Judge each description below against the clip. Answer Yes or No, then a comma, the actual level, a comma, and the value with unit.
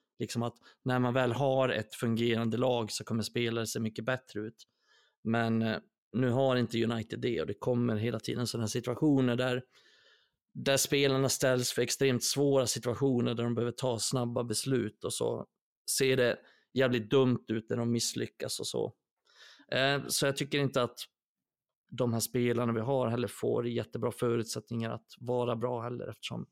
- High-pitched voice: No, low, 120 Hz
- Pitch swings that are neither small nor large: No, narrow, 2.0 semitones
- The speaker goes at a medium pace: Yes, average, 165 wpm